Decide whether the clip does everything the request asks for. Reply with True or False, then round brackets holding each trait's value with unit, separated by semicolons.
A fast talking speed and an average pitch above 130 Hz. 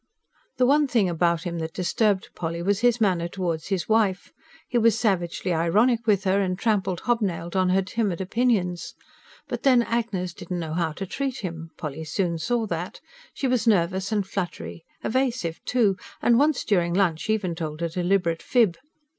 False (175 wpm; 190 Hz)